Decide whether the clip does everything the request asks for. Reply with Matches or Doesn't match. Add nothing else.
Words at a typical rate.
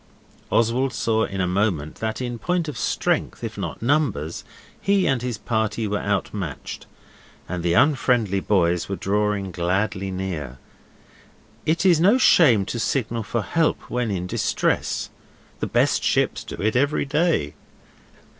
Matches